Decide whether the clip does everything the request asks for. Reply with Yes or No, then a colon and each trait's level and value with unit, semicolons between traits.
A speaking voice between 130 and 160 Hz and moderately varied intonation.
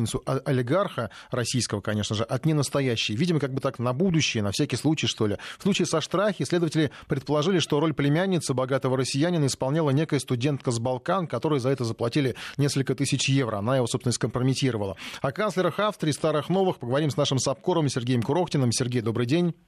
Yes: low, 135 Hz; average, 3.8 semitones